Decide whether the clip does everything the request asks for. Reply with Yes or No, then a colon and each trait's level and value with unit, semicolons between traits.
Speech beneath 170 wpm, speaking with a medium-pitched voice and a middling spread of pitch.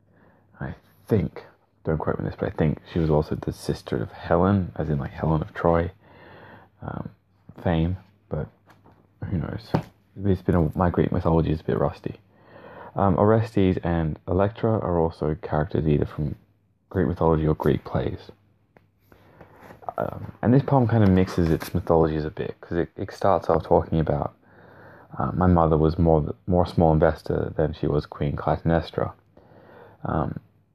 No: average, 160 wpm; very low, 90 Hz; average, 3.6 semitones